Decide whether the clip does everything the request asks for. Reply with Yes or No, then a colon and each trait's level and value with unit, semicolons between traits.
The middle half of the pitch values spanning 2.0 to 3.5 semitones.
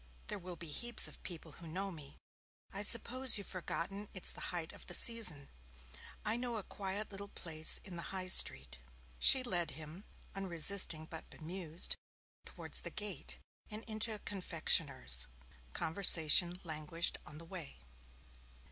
No: average, 4.1 semitones